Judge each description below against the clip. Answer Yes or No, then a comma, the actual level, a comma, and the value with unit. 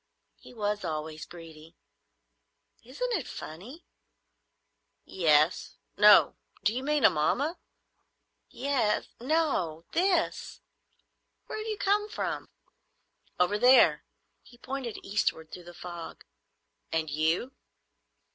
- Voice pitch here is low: No, high, 210 Hz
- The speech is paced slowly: Yes, slow, 100 wpm